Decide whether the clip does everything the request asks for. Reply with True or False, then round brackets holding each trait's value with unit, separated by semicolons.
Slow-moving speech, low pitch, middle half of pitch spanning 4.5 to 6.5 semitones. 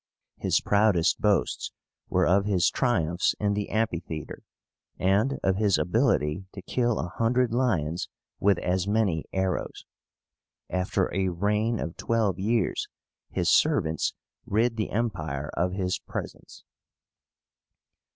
False (120 wpm; 100 Hz; 3.7 semitones)